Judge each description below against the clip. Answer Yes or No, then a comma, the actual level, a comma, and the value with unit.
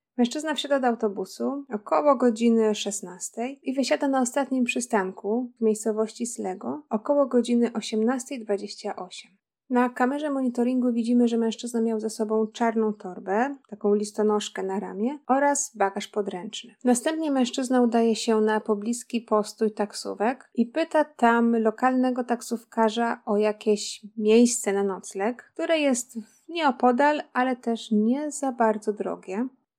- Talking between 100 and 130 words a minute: Yes, average, 125 wpm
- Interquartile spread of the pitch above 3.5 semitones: No, average, 3.1 semitones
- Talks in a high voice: Yes, high, 230 Hz